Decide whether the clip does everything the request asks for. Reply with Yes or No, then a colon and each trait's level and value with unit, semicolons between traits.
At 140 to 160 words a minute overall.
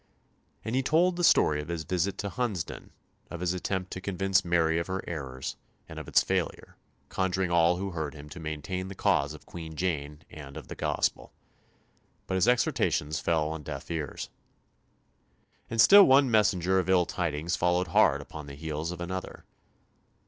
No: average, 180 wpm